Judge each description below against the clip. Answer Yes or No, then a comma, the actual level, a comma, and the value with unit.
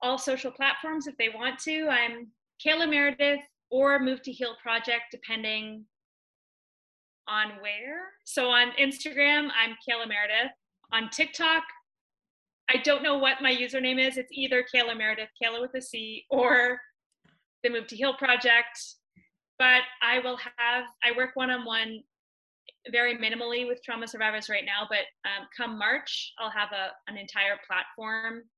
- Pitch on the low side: No, high, 245 Hz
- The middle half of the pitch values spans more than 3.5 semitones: No, average, 2.9 semitones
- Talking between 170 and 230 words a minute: No, average, 155 wpm